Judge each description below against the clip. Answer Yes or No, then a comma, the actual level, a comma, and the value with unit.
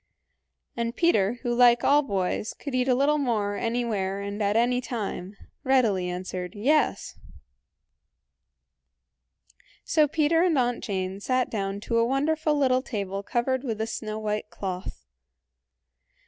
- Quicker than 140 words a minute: No, slow, 135 wpm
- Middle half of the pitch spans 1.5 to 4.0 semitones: No, average, 4.5 semitones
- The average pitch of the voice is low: No, high, 235 Hz